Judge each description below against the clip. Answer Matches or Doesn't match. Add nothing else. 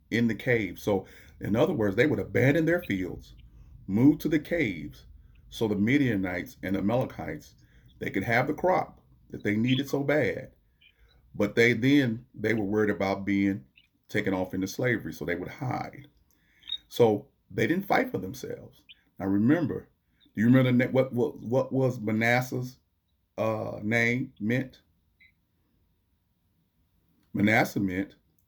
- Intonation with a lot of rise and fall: Matches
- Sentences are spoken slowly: Doesn't match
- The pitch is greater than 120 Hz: Doesn't match